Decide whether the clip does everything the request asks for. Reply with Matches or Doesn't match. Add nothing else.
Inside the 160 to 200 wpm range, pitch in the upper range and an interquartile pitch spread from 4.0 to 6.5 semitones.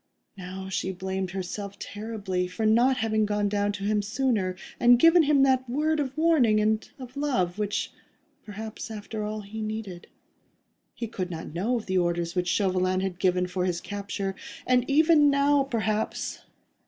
Matches